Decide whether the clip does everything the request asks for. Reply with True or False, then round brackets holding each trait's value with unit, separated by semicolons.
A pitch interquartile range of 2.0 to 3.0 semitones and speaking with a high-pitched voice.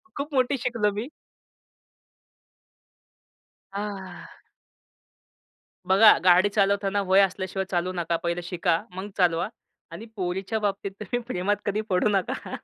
True (2.4 semitones; 195 Hz)